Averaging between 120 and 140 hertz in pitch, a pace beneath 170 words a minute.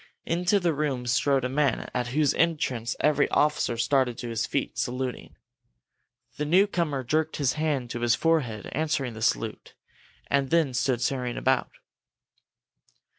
Yes: low, 135 Hz; average, 145 wpm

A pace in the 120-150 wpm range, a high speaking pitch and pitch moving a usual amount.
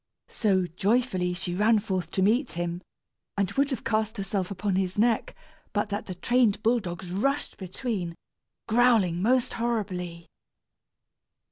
Yes: average, 140 wpm; high, 200 Hz; average, 4.2 semitones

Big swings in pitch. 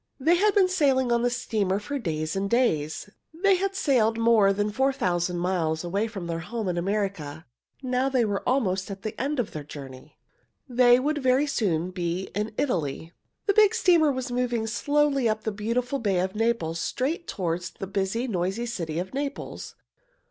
Yes: wide, 6.2 semitones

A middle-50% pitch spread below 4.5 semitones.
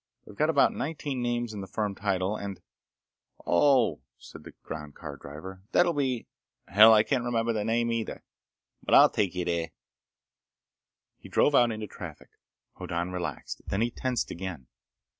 No: average, 4.8 semitones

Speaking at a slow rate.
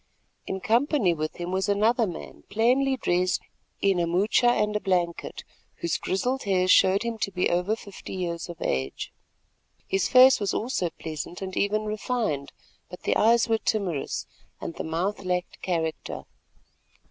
No: average, 160 wpm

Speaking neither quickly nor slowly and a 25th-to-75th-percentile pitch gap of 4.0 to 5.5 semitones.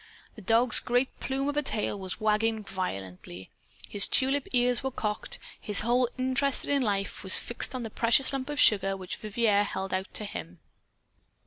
Yes: average, 180 wpm; average, 4.7 semitones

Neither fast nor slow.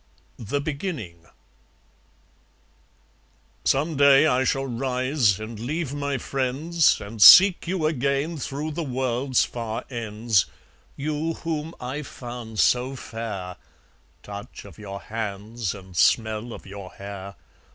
No: slow, 120 wpm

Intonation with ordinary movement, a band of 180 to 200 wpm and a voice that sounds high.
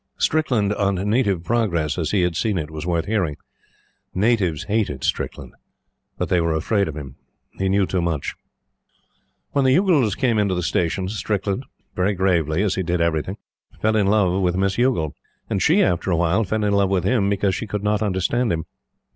No: average, 3.7 semitones; average, 190 wpm; very low, 95 Hz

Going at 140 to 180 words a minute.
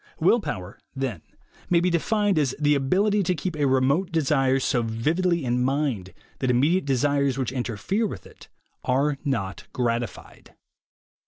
Yes: average, 150 wpm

